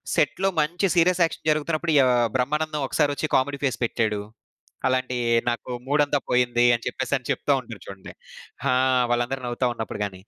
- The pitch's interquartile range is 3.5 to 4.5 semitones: Yes, average, 4.0 semitones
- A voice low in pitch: Yes, low, 130 Hz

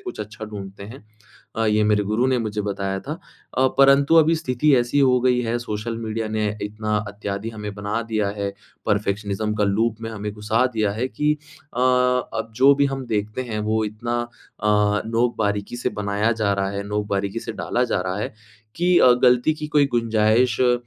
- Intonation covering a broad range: No, average, 3.2 semitones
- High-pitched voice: No, low, 110 Hz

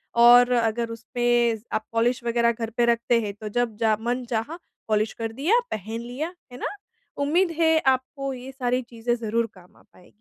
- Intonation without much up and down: Yes, narrow, 1.9 semitones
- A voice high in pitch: Yes, high, 235 Hz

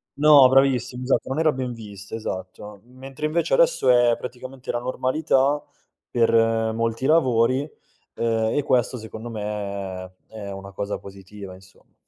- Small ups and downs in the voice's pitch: No, average, 4.3 semitones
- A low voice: Yes, low, 120 Hz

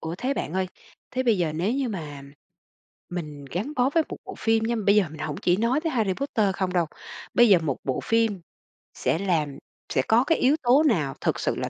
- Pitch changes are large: Yes, wide, 6.9 semitones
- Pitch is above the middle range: Yes, high, 200 Hz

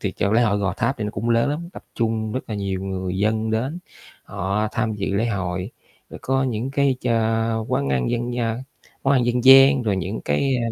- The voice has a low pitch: Yes, low, 110 Hz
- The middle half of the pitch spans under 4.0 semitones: Yes, average, 3.6 semitones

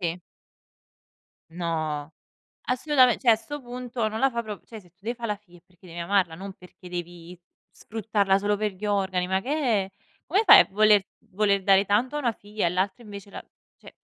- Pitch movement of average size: Yes, average, 3.7 semitones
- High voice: Yes, high, 200 Hz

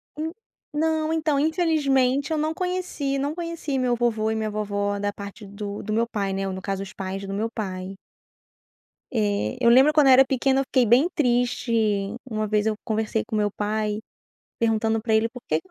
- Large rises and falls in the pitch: No, average, 5.0 semitones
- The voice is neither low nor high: No, high, 230 Hz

